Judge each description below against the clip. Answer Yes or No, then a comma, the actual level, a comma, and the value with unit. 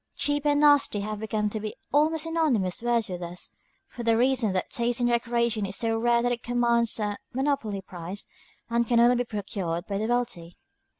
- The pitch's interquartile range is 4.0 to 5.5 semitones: No, average, 3.0 semitones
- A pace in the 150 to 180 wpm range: No, average, 195 wpm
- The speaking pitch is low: No, high, 235 Hz